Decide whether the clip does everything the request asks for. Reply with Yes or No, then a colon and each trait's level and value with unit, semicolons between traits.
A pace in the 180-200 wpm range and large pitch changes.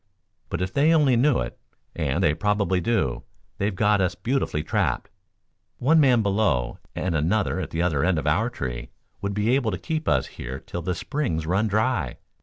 Yes: average, 190 wpm; wide, 6.5 semitones